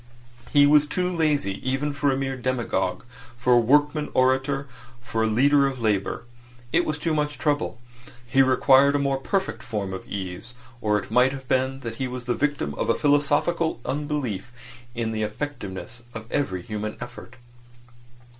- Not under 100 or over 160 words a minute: No, average, 170 wpm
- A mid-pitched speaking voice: No, low, 130 Hz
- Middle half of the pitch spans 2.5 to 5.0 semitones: Yes, average, 4.4 semitones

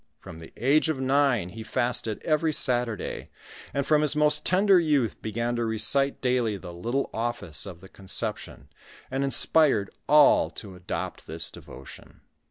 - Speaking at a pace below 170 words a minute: Yes, average, 155 wpm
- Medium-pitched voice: No, low, 120 Hz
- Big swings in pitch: Yes, wide, 5.8 semitones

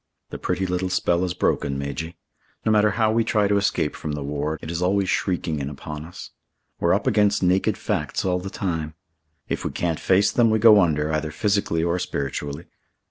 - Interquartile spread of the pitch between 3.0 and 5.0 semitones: Yes, average, 4.5 semitones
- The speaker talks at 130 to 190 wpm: No, average, 200 wpm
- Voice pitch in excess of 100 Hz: No, very low, 90 Hz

